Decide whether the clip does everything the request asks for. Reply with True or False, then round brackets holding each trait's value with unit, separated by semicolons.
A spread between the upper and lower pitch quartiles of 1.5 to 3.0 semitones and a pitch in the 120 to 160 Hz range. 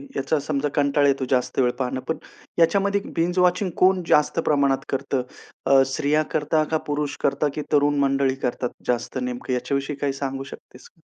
True (2.4 semitones; 140 Hz)